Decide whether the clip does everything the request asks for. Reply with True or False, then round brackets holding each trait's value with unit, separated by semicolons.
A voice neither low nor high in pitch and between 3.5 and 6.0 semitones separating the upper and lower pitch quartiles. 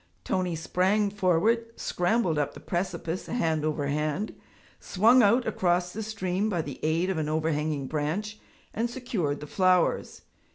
True (180 Hz; 5.1 semitones)